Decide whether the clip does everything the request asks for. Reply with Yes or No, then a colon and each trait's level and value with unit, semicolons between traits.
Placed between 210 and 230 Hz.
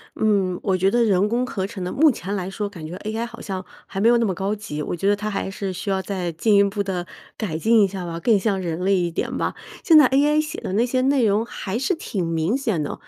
No: high, 200 Hz